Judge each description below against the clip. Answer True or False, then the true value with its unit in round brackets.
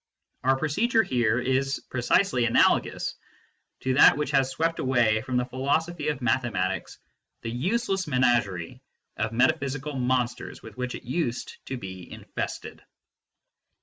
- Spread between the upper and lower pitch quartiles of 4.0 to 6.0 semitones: False (3.6 semitones)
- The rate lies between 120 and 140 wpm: True (135 wpm)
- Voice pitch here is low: True (130 Hz)